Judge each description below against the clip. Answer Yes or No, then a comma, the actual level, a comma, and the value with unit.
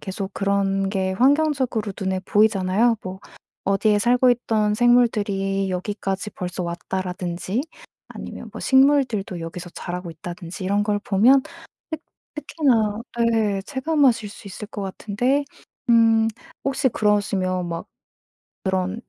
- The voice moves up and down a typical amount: Yes, average, 3.9 semitones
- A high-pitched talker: Yes, high, 205 Hz